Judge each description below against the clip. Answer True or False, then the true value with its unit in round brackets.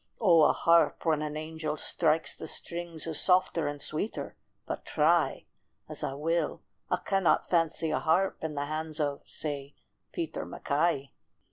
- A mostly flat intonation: True (2.0 semitones)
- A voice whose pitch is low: False (160 Hz)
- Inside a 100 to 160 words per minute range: True (155 wpm)